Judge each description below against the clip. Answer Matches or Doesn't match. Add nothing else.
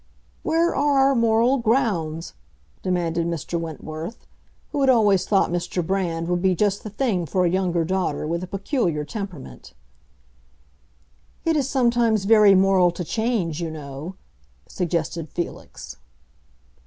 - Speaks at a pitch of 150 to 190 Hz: Matches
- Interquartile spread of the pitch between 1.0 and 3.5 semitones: Doesn't match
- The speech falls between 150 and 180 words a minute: Doesn't match